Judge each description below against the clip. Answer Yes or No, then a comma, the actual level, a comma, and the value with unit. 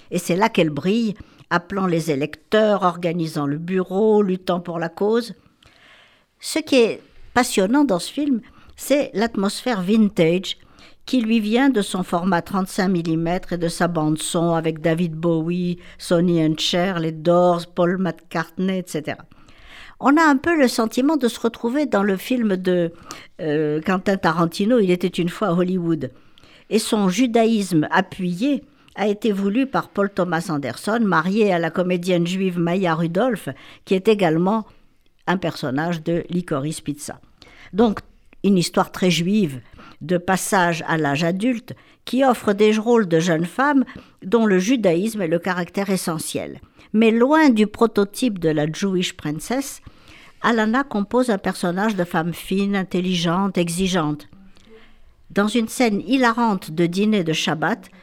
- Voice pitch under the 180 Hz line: No, medium, 185 Hz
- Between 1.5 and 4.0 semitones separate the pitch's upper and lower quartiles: No, average, 4.6 semitones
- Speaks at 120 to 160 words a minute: Yes, average, 150 wpm